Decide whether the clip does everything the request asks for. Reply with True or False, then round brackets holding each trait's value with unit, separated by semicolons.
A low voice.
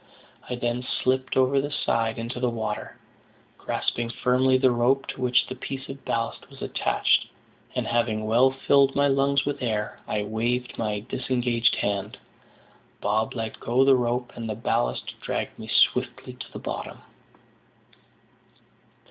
True (120 Hz)